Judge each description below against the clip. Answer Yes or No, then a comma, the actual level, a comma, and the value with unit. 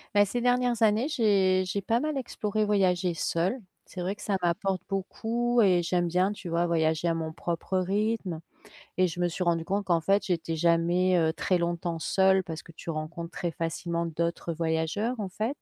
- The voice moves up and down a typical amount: Yes, average, 3.5 semitones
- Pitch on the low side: No, medium, 180 Hz